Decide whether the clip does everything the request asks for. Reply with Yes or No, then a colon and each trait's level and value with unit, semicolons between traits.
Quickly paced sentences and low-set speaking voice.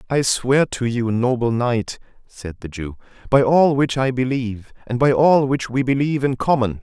No: average, 195 wpm; low, 125 Hz